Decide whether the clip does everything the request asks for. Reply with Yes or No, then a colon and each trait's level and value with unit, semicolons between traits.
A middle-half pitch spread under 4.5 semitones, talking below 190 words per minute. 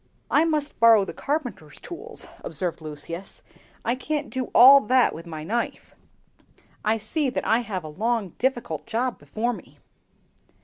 No: wide, 5.6 semitones; average, 150 wpm